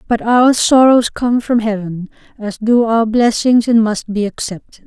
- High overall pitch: Yes, high, 225 Hz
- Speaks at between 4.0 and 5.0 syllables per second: Yes, 4.3 syllables/s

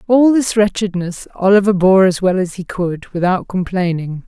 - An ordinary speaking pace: Yes, average, 170 wpm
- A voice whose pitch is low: No, high, 190 Hz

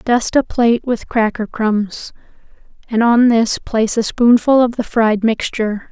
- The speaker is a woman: Yes, female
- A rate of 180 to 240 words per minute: No, average, 160 wpm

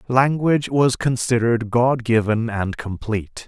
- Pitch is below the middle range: Yes, low, 120 Hz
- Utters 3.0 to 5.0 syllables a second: Yes, 4.5 syllables/s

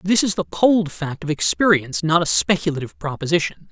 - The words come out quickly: No, average, 180 wpm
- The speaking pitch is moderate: Yes, medium, 165 Hz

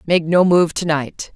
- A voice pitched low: No, medium, 165 Hz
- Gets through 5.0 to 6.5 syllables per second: No, 4.1 syllables/s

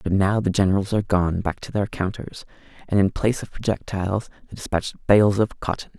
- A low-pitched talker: Yes, low, 100 Hz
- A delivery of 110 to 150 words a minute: No, average, 200 wpm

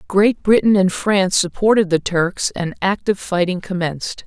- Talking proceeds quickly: No, average, 155 wpm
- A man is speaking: No, female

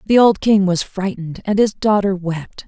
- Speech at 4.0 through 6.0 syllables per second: Yes, 4.9 syllables/s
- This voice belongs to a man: No, female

